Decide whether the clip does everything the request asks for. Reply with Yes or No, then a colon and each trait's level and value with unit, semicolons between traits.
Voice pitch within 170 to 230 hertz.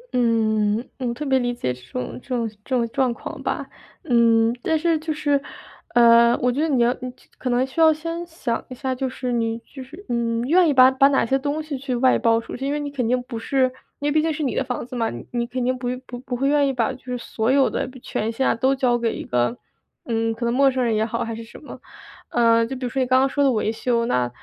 No: very high, 250 Hz